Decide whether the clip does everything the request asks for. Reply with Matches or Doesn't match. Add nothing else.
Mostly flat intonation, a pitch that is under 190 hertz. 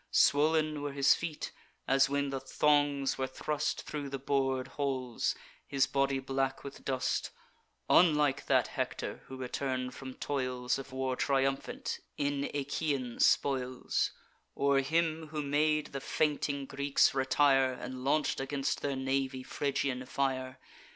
Matches